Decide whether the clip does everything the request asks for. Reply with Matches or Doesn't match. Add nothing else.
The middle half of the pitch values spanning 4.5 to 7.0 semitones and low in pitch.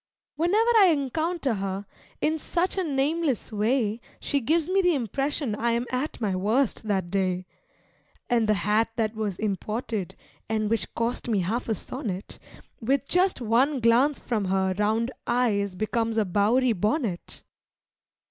Doesn't match